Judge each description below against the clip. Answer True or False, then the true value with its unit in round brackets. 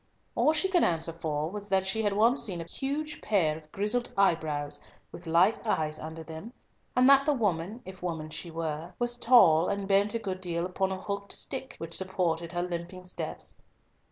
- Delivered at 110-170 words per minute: False (195 wpm)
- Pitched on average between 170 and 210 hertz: True (185 Hz)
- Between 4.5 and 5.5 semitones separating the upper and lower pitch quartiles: True (4.8 semitones)